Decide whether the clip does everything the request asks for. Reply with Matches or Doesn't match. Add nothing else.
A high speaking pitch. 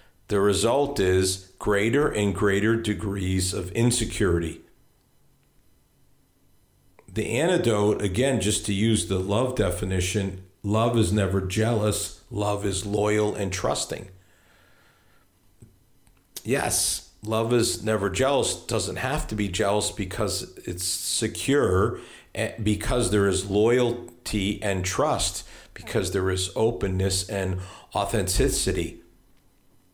Doesn't match